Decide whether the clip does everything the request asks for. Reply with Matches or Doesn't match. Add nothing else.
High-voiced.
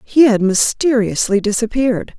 Matches